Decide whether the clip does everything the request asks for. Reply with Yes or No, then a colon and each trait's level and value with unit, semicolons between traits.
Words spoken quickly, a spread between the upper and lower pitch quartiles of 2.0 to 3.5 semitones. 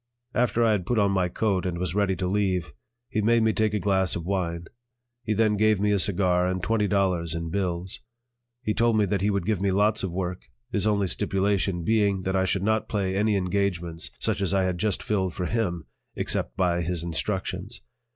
Yes: fast, 215 wpm; narrow, 2.5 semitones